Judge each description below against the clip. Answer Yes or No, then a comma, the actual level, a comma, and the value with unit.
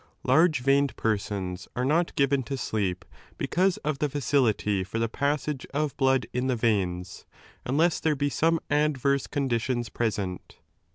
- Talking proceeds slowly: No, average, 165 wpm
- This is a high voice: No, low, 130 Hz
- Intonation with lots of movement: No, average, 5.0 semitones